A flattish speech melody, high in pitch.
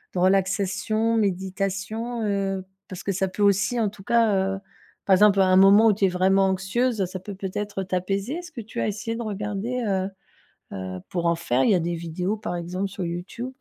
Yes: narrow, 2.3 semitones; high, 195 Hz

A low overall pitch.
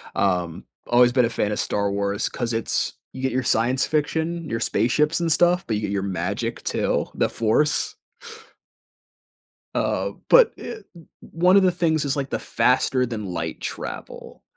Yes: low, 125 Hz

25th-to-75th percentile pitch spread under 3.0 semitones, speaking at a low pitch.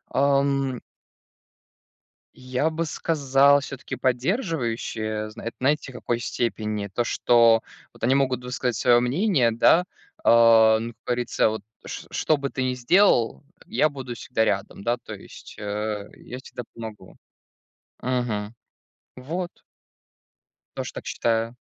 No: average, 3.4 semitones; low, 125 Hz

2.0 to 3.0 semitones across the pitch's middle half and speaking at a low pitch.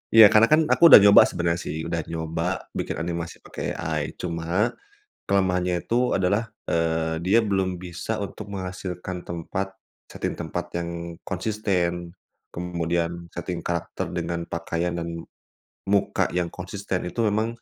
Yes: average, 2.7 semitones; very low, 90 Hz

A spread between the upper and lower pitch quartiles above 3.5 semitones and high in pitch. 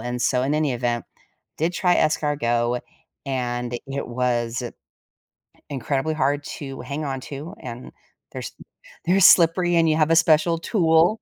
No: average, 4.7 semitones; medium, 145 Hz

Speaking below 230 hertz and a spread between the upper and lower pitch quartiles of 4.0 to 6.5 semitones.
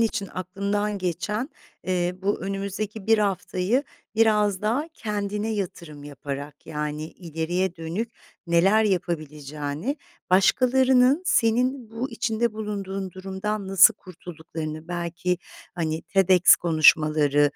Yes: high, 190 Hz; average, 4.4 semitones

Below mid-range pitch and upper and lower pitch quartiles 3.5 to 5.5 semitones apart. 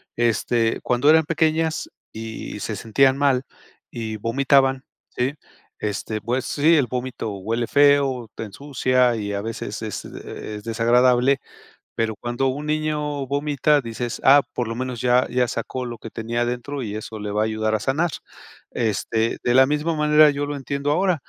Yes: low, 125 Hz; average, 4.0 semitones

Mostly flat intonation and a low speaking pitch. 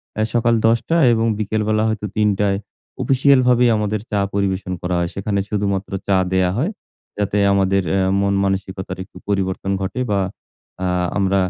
Yes: narrow, 2.1 semitones; low, 100 Hz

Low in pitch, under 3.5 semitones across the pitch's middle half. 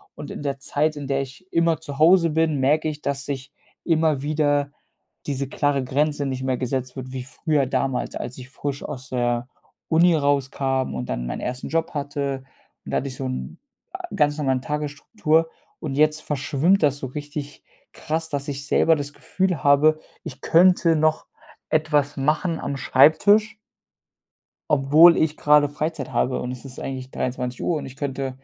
No: medium, 145 Hz; average, 2.7 semitones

